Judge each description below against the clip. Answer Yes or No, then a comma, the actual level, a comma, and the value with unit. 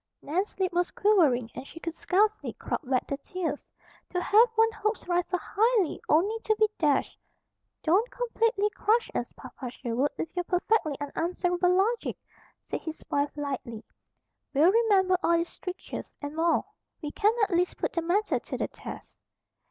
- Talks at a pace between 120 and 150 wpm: No, average, 165 wpm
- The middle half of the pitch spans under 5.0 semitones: No, wide, 5.6 semitones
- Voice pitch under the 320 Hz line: No, very high, 360 Hz